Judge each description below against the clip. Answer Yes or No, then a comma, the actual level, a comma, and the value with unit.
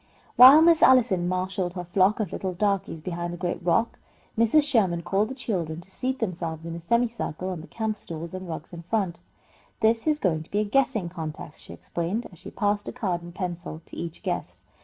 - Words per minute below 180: No, fast, 205 wpm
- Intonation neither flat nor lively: Yes, average, 4.6 semitones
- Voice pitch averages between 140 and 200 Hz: Yes, medium, 185 Hz